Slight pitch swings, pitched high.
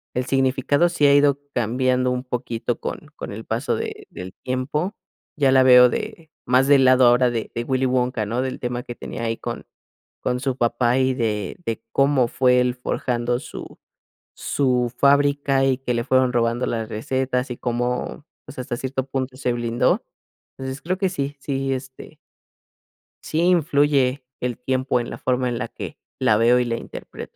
No: narrow, 1.8 semitones; low, 130 Hz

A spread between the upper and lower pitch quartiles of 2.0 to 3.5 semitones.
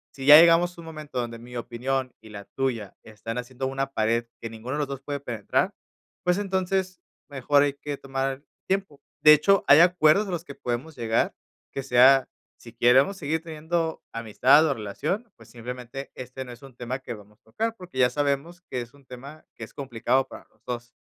No: average, 4.4 semitones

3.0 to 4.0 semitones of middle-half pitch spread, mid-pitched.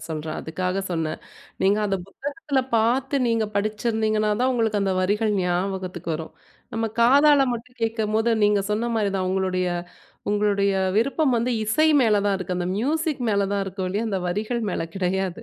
No: average, 3.5 semitones; high, 210 Hz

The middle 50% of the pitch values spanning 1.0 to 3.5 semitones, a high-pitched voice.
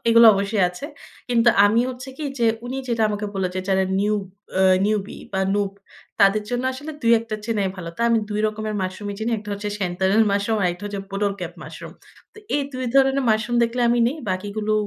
Yes: average, 2.9 semitones; high, 215 Hz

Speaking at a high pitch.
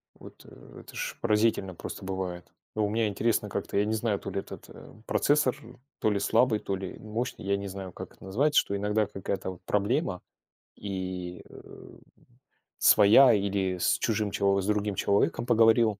No: low, 100 Hz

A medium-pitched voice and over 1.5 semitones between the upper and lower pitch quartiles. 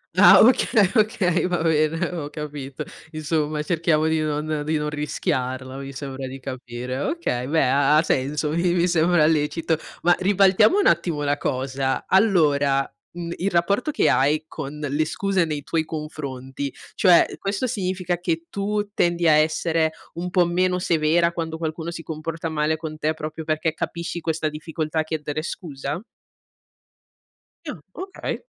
Yes: medium, 160 Hz; average, 2.7 semitones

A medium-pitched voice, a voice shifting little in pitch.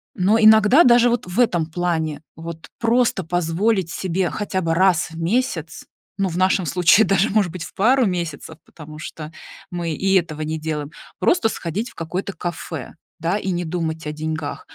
No: medium, 175 Hz; average, 3.8 semitones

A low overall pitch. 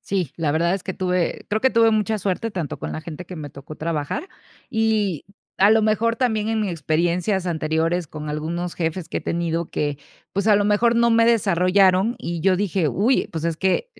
No: medium, 185 Hz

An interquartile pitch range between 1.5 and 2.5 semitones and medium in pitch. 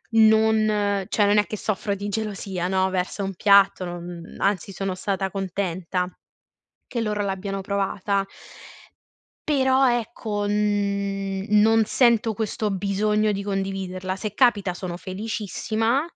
No: narrow, 1.9 semitones; high, 200 Hz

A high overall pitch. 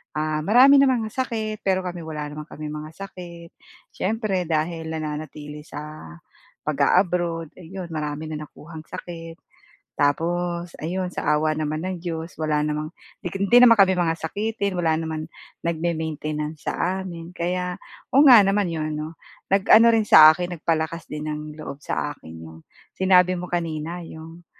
No: medium, 165 Hz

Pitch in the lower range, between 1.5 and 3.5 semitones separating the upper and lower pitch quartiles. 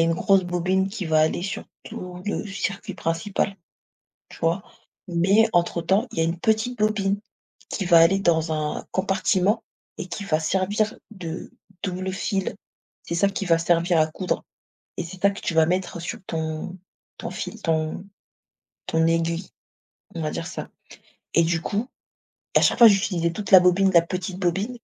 No: medium, 180 Hz; average, 2.9 semitones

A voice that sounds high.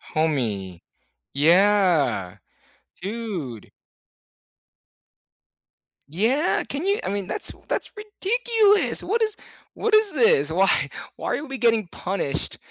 Yes: high, 205 Hz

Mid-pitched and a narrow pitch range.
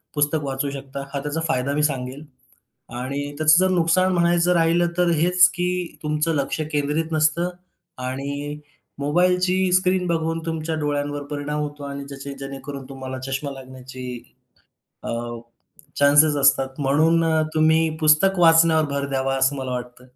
No: medium, 150 Hz; average, 3.1 semitones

